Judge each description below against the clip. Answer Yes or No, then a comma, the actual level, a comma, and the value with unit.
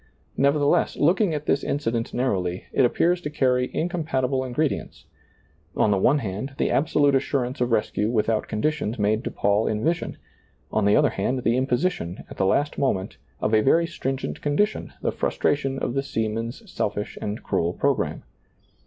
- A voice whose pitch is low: Yes, low, 130 Hz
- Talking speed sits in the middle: Yes, average, 175 wpm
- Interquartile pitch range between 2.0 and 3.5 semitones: No, average, 5.1 semitones